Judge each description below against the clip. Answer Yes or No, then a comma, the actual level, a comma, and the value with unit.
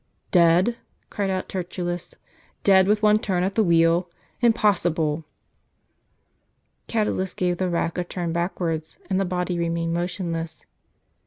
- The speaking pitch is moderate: Yes, medium, 180 Hz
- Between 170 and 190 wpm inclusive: No, average, 145 wpm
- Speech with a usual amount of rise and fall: No, narrow, 2.1 semitones